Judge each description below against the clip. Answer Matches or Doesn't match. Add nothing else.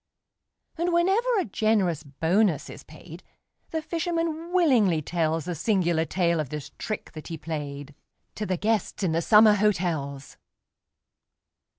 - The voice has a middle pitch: Matches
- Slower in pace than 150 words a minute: Matches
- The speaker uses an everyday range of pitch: Doesn't match